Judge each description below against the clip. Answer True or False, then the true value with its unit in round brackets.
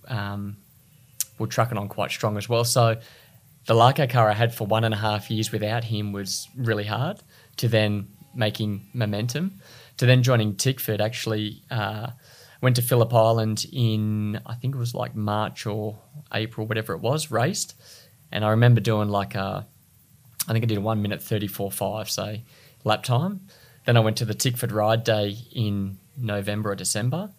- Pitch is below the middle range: True (115 Hz)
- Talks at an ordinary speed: True (185 wpm)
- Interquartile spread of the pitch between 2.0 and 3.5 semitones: True (2.8 semitones)